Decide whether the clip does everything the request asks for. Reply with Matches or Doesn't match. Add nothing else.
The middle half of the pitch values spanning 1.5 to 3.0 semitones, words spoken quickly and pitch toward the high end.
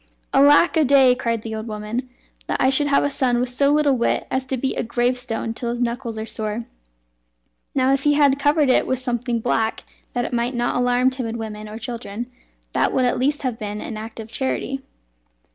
Matches